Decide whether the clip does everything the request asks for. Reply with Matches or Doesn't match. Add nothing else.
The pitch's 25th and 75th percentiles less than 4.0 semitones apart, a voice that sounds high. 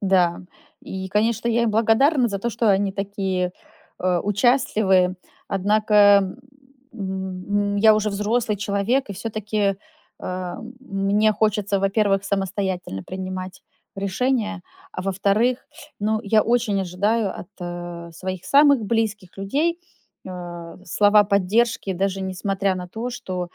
Matches